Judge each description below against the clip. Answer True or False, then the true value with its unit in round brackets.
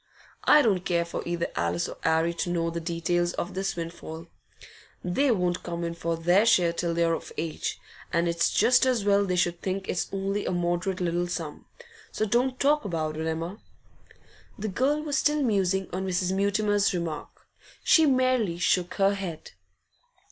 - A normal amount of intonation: True (3.2 semitones)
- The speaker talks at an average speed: True (175 wpm)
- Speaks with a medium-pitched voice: True (180 Hz)